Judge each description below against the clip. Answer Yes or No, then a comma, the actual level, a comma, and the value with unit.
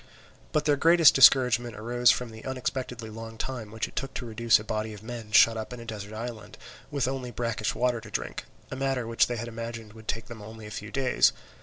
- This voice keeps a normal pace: No, fast, 225 wpm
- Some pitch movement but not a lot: No, narrow, 2.2 semitones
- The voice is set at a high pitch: No, low, 115 Hz